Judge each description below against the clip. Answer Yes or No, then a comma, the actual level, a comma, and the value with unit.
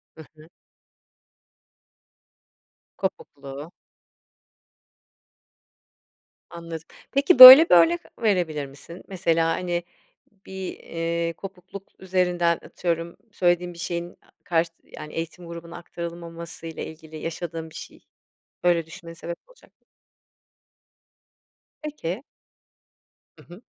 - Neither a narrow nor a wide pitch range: No, narrow, 1.5 semitones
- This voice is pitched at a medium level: Yes, medium, 170 Hz